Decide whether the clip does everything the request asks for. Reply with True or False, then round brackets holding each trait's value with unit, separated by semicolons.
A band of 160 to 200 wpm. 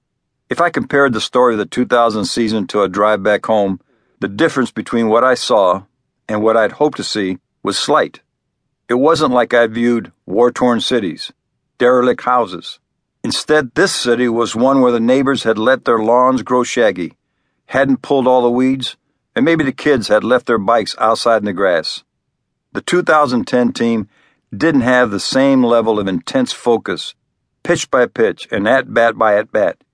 True (175 wpm)